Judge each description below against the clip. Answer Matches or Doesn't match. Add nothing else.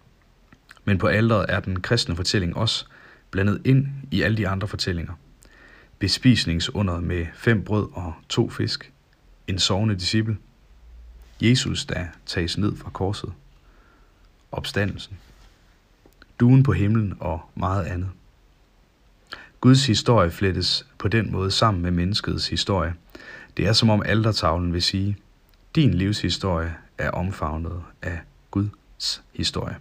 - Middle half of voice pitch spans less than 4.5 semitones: Matches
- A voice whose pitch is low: Matches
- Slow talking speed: Matches